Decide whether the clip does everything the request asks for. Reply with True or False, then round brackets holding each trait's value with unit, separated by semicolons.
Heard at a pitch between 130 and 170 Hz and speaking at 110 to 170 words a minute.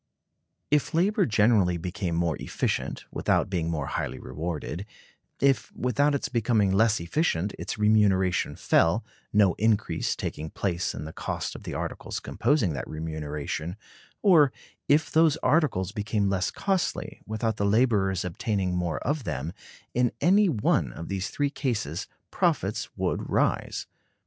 False (100 Hz; 140 wpm)